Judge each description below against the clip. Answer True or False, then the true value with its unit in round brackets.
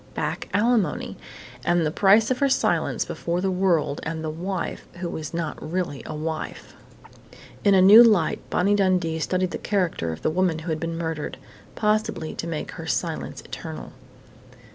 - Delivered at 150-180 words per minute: True (170 wpm)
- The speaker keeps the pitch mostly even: False (3.5 semitones)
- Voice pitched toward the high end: False (175 Hz)